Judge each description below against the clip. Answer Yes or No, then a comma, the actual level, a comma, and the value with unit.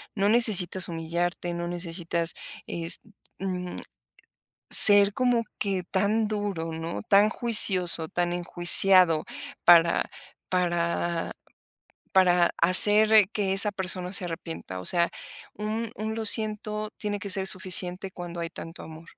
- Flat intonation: No, average, 3.2 semitones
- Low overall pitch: No, medium, 185 Hz